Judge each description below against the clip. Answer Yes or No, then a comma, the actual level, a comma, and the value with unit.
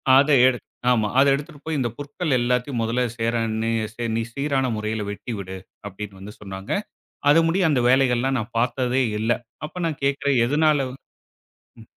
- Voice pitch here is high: No, low, 125 Hz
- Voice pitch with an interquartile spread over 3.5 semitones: Yes, average, 4.0 semitones